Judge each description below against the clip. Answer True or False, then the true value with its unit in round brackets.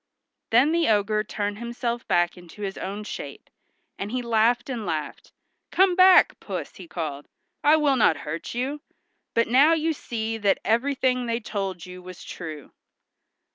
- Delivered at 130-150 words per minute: False (160 wpm)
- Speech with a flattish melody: False (5.0 semitones)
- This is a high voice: True (225 Hz)